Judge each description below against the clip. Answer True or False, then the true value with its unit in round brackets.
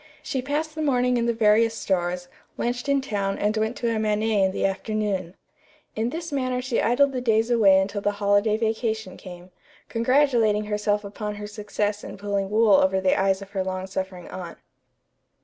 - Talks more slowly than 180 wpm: False (185 wpm)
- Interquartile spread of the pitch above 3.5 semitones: False (3.2 semitones)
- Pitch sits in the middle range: False (210 Hz)